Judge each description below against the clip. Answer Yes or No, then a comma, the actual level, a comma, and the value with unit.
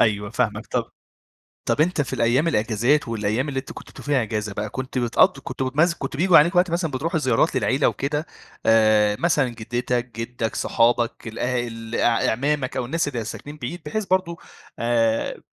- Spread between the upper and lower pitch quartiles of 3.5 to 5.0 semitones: Yes, average, 4.6 semitones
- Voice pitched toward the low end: Yes, low, 125 Hz